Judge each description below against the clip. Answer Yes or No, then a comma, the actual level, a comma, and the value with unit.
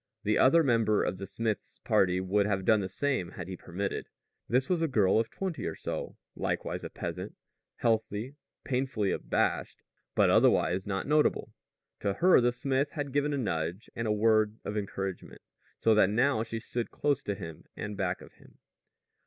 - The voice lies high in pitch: No, low, 110 Hz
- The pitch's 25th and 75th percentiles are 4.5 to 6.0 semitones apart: Yes, average, 5.2 semitones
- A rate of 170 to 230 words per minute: Yes, average, 180 wpm